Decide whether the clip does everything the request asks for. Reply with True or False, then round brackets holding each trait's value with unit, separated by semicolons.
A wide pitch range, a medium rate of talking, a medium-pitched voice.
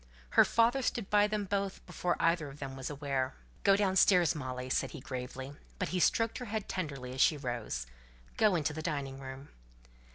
True (6.7 semitones; 190 wpm; 155 Hz)